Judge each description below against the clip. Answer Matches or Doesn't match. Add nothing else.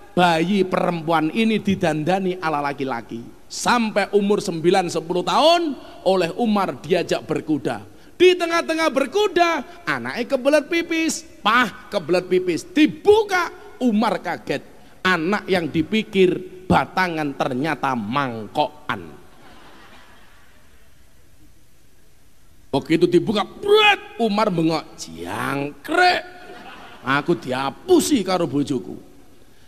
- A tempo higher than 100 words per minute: Doesn't match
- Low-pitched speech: Doesn't match